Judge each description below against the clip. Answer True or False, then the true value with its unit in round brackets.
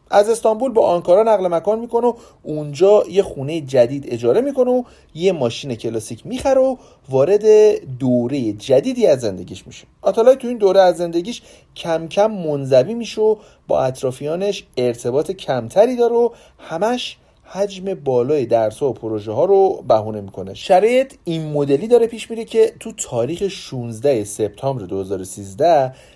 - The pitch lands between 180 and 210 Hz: False (170 Hz)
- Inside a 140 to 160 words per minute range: True (150 wpm)